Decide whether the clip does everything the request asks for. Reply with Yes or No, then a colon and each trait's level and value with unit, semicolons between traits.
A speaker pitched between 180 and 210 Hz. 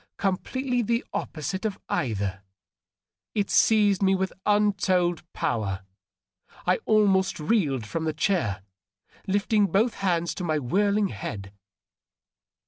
Yes: high, 190 Hz